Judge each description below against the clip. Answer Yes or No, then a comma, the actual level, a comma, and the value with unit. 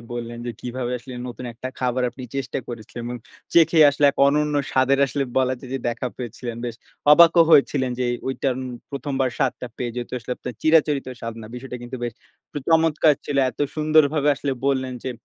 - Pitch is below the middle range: Yes, low, 130 Hz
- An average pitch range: Yes, average, 3.0 semitones